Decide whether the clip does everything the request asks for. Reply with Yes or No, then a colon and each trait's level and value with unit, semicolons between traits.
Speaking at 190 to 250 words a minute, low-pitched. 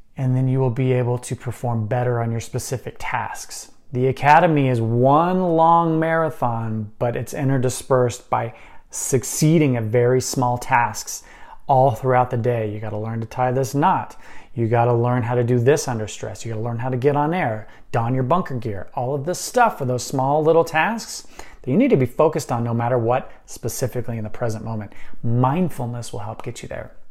Yes: average, 200 wpm; low, 125 Hz